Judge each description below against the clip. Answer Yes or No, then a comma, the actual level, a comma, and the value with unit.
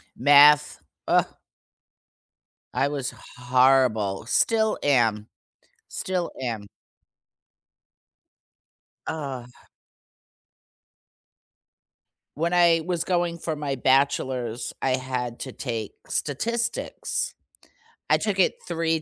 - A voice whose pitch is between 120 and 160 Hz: Yes, medium, 140 Hz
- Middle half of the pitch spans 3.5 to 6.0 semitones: Yes, average, 5.1 semitones